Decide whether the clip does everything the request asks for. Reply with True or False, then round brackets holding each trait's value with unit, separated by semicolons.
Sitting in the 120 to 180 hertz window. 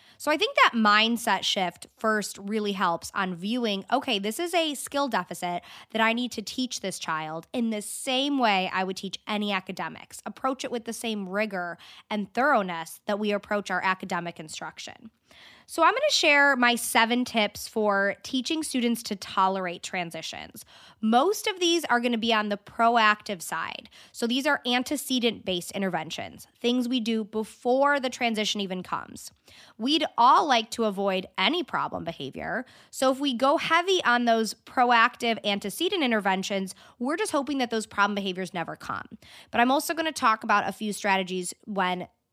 False (220 Hz)